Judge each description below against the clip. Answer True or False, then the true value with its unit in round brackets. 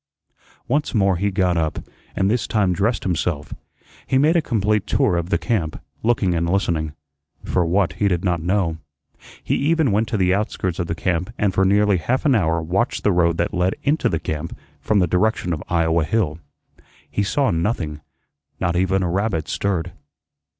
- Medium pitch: False (95 Hz)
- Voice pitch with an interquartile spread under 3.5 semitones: False (3.8 semitones)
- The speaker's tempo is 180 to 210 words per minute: True (185 wpm)